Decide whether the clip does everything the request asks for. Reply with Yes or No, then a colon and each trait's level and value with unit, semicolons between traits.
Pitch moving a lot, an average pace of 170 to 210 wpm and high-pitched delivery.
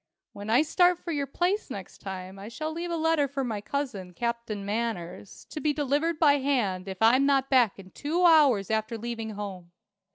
Yes: wide, 6.6 semitones; average, 195 wpm; high, 245 Hz